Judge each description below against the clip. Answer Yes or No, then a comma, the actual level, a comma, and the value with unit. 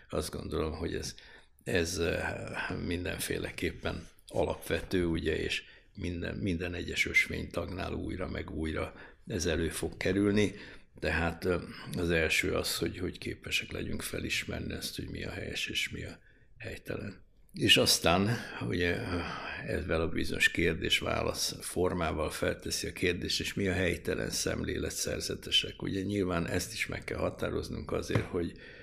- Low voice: Yes, very low, 90 Hz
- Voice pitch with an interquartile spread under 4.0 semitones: Yes, average, 2.7 semitones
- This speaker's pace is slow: No, average, 135 wpm